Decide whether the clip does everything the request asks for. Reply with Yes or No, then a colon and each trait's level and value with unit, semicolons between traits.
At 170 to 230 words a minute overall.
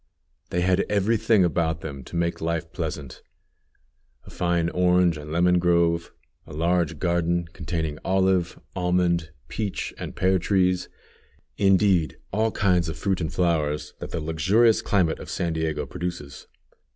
No: average, 145 wpm